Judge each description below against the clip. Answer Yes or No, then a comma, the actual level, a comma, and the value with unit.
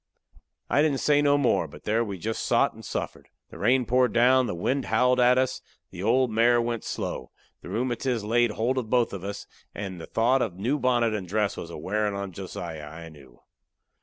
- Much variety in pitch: No, average, 4.4 semitones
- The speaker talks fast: Yes, fast, 215 wpm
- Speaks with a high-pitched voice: No, low, 115 Hz